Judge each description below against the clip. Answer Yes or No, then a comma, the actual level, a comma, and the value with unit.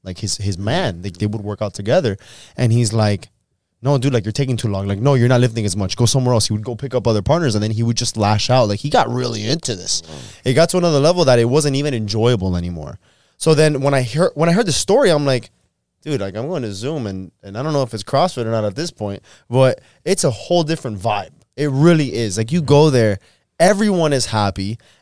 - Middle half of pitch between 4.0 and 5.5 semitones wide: Yes, average, 5.1 semitones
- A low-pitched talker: Yes, low, 120 Hz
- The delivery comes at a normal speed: No, fast, 260 wpm